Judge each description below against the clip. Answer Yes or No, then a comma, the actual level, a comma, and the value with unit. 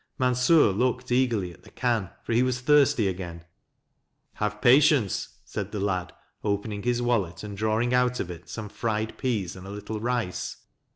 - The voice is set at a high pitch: No, low, 110 Hz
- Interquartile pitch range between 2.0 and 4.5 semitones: Yes, average, 4.1 semitones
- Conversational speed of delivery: Yes, average, 175 wpm